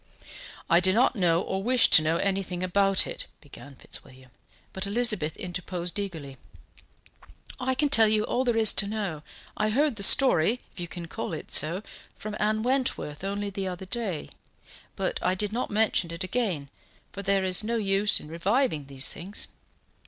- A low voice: No, high, 195 Hz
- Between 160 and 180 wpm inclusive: Yes, average, 175 wpm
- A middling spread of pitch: Yes, average, 4.2 semitones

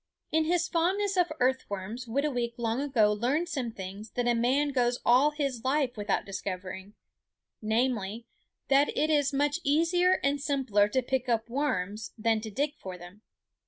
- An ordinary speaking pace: Yes, average, 160 wpm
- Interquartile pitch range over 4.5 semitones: Yes, average, 5.1 semitones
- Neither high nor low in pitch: No, very high, 250 Hz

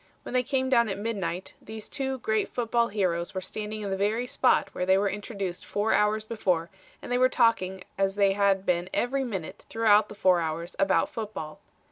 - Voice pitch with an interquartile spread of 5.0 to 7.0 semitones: No, average, 3.3 semitones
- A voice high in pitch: Yes, high, 205 Hz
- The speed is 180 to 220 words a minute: Yes, average, 200 wpm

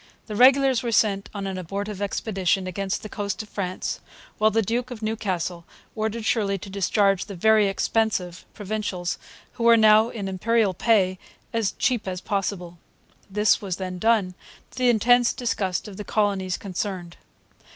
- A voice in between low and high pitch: No, high, 205 Hz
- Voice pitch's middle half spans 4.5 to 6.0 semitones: No, average, 2.8 semitones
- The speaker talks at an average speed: Yes, average, 160 wpm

